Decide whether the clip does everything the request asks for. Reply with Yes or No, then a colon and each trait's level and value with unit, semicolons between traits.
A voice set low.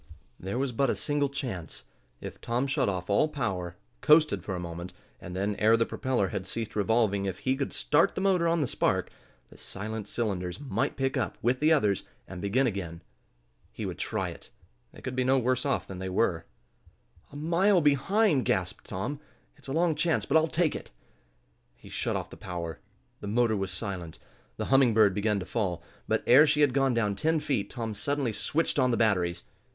Yes: low, 120 Hz